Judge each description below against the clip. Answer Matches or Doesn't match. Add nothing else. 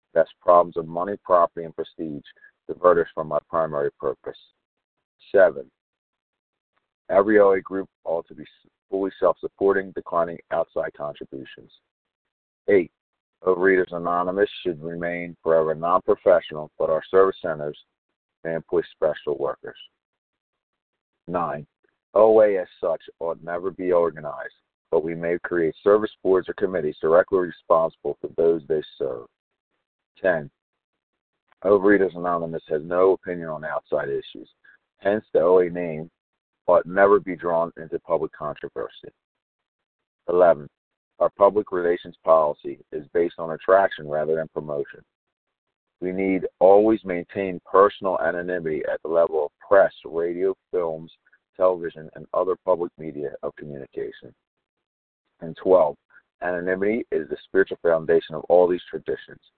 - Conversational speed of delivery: Doesn't match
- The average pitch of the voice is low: Matches